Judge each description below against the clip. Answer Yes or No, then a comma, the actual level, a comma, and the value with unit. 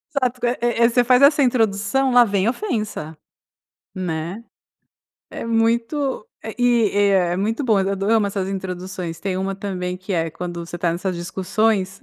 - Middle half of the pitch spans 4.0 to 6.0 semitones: Yes, average, 4.3 semitones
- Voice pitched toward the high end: Yes, high, 205 Hz